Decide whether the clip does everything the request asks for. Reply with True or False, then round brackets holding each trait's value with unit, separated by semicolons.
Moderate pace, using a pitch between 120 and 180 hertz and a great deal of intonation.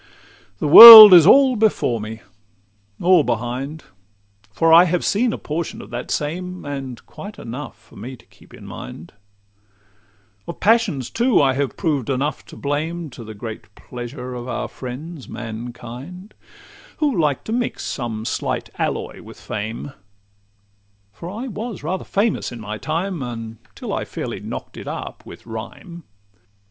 True (150 wpm; 140 Hz; 7.4 semitones)